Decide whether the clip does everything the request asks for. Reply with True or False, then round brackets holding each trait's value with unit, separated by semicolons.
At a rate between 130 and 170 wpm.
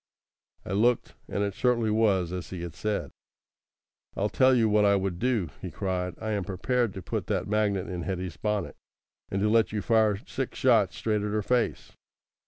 False (190 wpm)